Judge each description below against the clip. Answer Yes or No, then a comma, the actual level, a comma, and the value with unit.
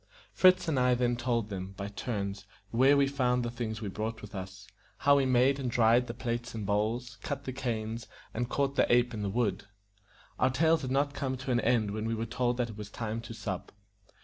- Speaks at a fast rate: Yes, fast, 230 wpm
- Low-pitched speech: Yes, low, 120 Hz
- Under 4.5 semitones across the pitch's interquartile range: Yes, average, 3.0 semitones